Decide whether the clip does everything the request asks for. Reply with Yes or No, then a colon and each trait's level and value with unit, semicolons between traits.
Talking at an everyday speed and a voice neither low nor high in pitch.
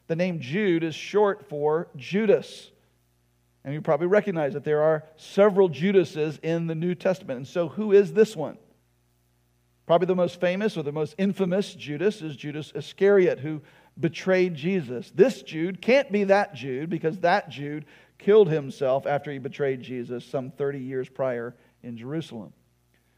Yes: average, 160 wpm; medium, 155 Hz